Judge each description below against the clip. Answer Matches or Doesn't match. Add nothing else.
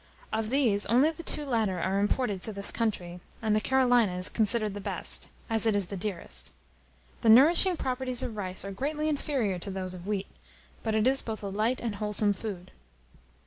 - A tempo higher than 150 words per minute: Matches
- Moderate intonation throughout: Matches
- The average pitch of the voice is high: Matches